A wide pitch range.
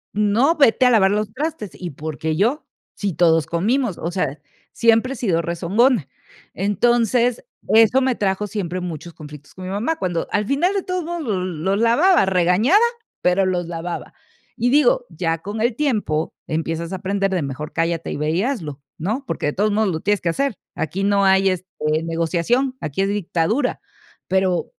Yes: wide, 5.7 semitones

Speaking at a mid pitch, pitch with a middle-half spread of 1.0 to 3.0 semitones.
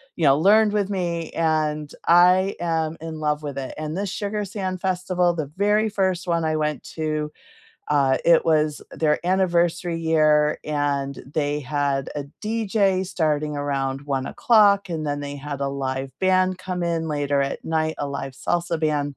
No: medium, 160 Hz; average, 4.0 semitones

